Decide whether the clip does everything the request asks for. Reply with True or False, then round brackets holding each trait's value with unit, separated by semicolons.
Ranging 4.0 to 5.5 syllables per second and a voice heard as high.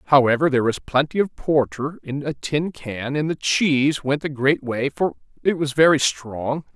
False (4.6 syllables/s; 140 Hz)